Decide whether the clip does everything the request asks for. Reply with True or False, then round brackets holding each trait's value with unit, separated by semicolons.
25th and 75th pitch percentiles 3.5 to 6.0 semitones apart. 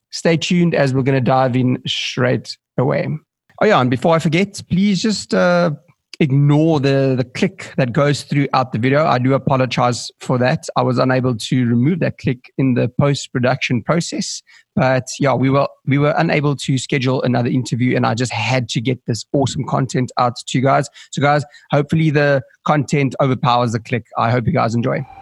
False (3.0 semitones)